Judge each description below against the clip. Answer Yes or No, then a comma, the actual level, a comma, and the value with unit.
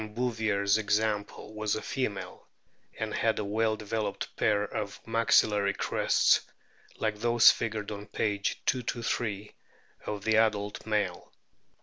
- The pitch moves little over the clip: Yes, narrow, 1.4 semitones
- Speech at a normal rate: No, slow, 120 wpm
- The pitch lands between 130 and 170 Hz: No, low, 105 Hz